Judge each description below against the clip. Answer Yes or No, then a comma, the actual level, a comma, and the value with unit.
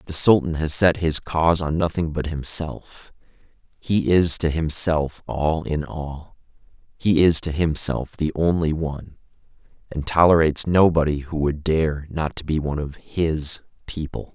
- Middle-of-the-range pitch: No, very low, 80 Hz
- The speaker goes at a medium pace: Yes, average, 155 wpm